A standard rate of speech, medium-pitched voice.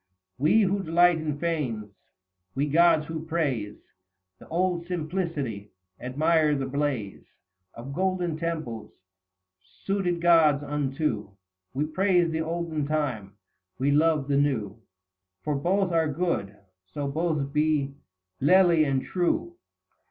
No: slow, 120 wpm; medium, 155 Hz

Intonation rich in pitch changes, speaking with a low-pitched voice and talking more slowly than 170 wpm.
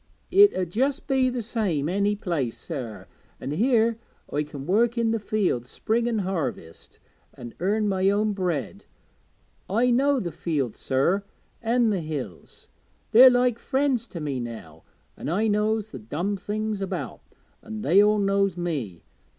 No: wide, 6.9 semitones; high, 200 Hz; average, 160 wpm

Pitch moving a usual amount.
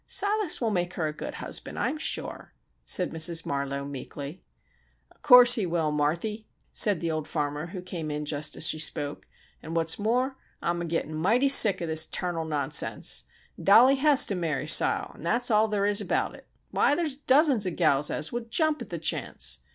No: wide, 7.2 semitones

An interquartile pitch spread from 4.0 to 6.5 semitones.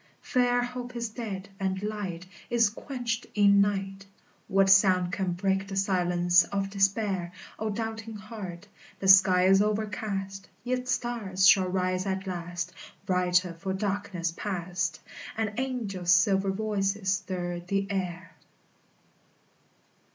No: narrow, 2.4 semitones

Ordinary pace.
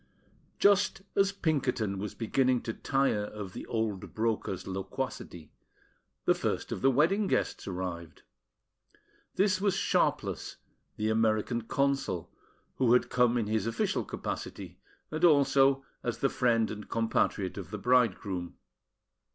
No: slow, 130 wpm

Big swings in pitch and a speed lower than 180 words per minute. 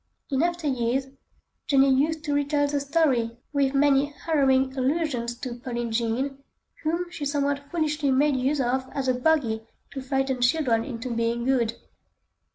No: average, 2.7 semitones; average, 155 wpm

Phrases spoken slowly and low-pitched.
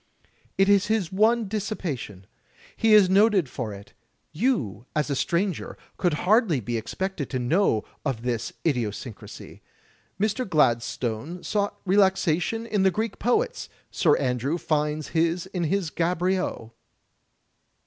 No: slow, 120 wpm; medium, 175 Hz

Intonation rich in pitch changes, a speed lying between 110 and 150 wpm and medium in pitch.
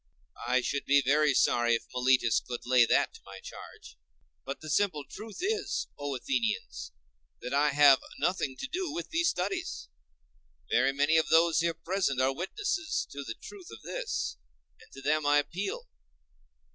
No: wide, 6.5 semitones; average, 170 wpm; medium, 145 Hz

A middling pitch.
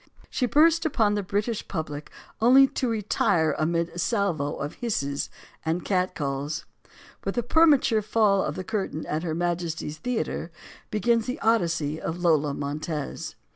Yes: medium, 180 Hz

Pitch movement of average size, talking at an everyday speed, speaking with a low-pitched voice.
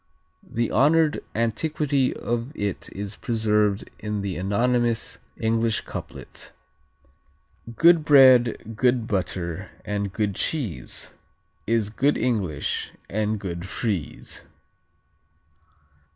No: average, 3.7 semitones; slow, 95 wpm; low, 110 Hz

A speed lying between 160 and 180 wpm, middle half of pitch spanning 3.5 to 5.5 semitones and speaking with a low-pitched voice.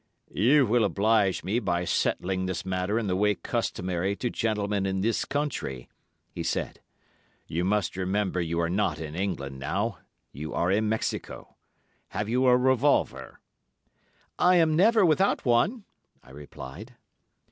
No: average, 145 wpm; average, 4.8 semitones; low, 100 Hz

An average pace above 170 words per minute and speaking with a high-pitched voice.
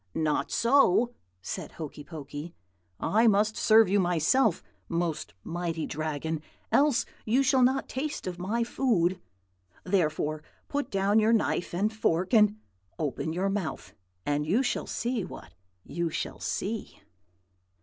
No: slow, 135 wpm; high, 195 Hz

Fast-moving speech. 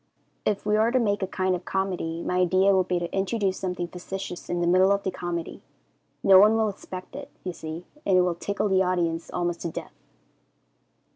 Yes: fast, 210 wpm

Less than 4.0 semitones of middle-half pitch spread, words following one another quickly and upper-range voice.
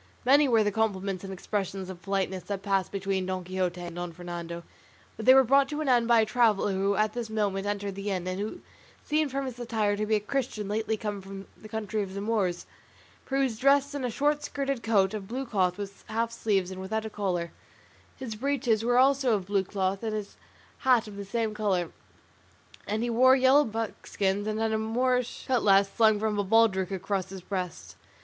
Yes: average, 3.5 semitones; fast, 215 wpm; high, 210 Hz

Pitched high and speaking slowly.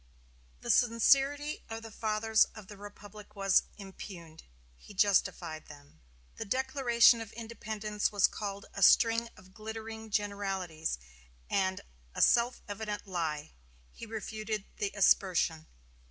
Yes: high, 210 Hz; slow, 125 wpm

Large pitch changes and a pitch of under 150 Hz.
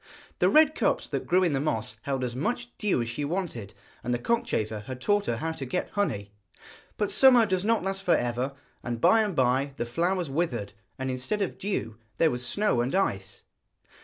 Yes: wide, 8.3 semitones; medium, 140 Hz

